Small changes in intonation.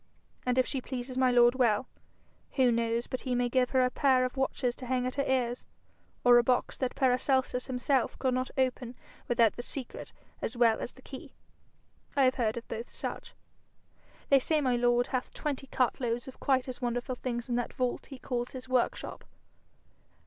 Yes: narrow, 1.3 semitones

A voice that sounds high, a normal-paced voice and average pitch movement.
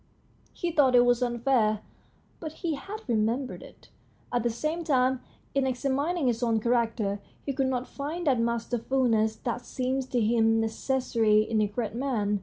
Yes: high, 245 Hz; average, 170 wpm; average, 3.2 semitones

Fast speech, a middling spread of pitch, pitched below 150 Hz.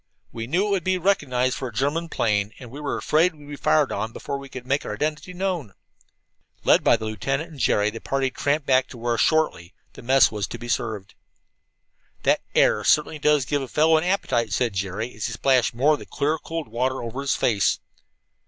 Yes: fast, 215 wpm; average, 4.8 semitones; low, 135 Hz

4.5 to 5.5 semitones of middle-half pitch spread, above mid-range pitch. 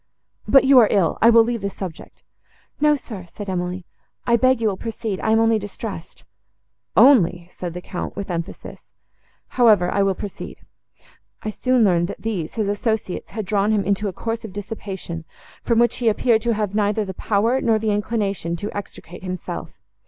No: average, 3.2 semitones; high, 205 Hz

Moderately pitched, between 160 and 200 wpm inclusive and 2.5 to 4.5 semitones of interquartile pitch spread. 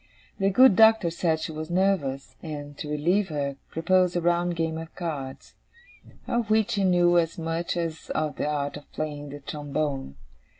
Yes: medium, 165 Hz; average, 175 wpm; average, 3.4 semitones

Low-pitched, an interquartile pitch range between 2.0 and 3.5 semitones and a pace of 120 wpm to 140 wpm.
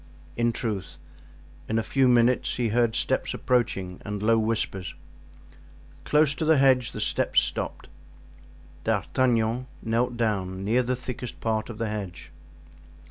Yes: low, 115 Hz; average, 2.8 semitones; slow, 135 wpm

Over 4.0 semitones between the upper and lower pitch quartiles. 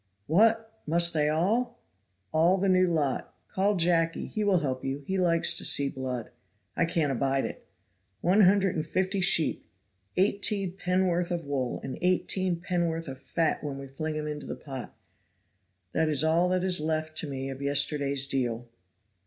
Yes: average, 4.6 semitones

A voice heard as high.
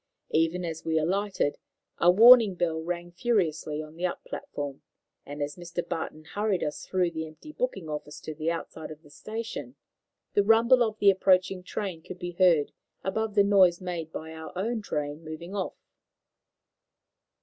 No: medium, 175 Hz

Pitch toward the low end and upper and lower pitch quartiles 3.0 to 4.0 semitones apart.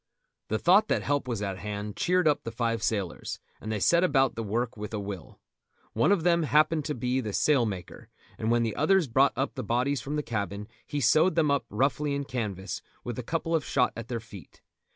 No: low, 125 Hz; wide, 5.5 semitones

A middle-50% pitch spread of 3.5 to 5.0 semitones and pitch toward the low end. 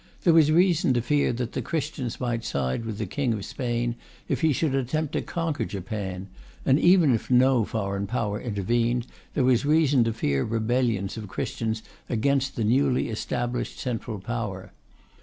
Yes: average, 3.8 semitones; low, 120 Hz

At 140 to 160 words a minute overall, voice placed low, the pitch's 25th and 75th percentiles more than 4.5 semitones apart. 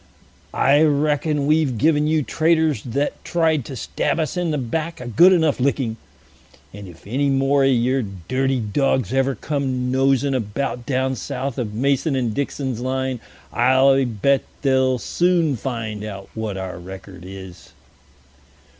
No: average, 150 wpm; low, 130 Hz; average, 3.8 semitones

